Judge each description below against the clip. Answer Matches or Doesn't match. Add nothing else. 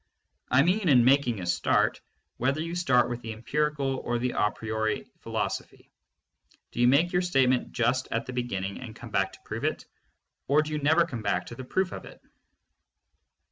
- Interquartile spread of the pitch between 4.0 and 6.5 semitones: Matches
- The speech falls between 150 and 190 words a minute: Doesn't match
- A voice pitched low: Matches